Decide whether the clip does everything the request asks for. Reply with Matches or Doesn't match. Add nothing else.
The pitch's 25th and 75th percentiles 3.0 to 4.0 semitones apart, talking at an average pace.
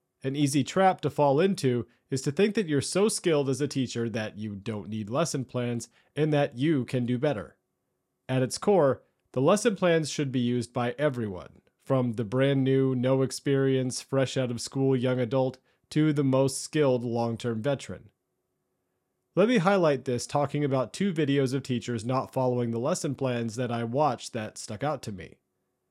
Matches